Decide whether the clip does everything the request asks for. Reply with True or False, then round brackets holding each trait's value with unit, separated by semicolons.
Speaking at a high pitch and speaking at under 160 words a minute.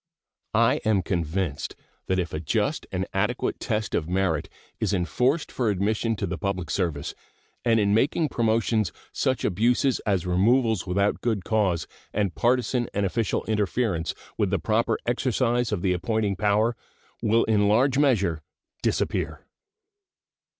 False (105 Hz; 145 wpm)